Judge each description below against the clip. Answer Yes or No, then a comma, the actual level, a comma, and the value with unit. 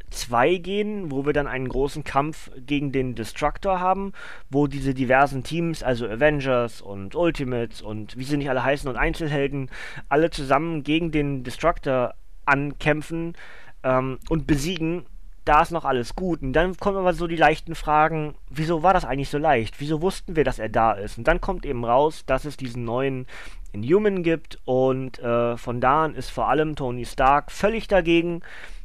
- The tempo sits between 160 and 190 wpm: Yes, average, 180 wpm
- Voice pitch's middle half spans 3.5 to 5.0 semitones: Yes, average, 4.2 semitones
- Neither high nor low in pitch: Yes, medium, 145 Hz